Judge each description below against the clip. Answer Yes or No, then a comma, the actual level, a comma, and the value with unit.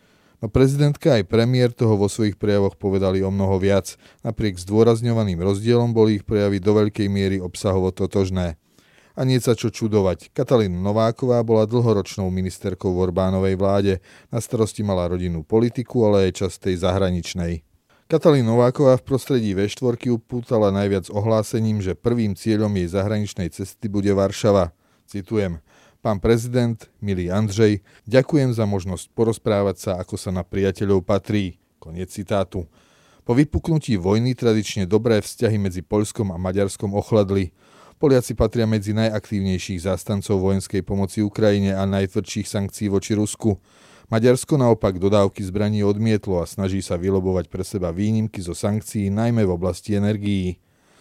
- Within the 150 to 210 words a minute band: No, average, 140 wpm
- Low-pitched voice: Yes, low, 105 Hz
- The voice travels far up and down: No, average, 2.8 semitones